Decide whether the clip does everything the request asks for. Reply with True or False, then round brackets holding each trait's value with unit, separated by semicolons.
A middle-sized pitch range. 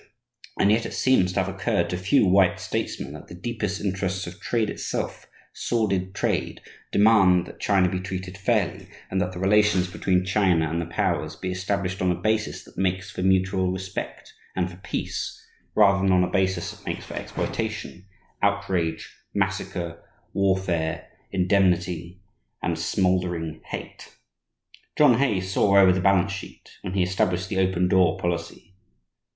False (1.5 semitones)